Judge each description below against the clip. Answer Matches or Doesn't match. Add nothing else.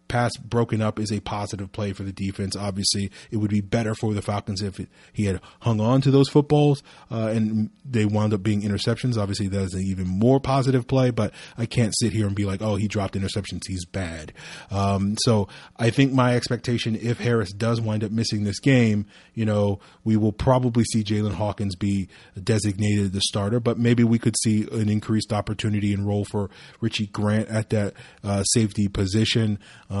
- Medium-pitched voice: Doesn't match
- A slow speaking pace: Doesn't match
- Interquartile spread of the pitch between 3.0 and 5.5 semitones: Doesn't match